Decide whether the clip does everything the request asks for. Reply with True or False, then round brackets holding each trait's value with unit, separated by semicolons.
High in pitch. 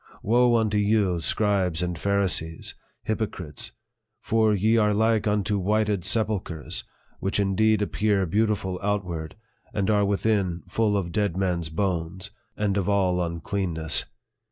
False (100 Hz)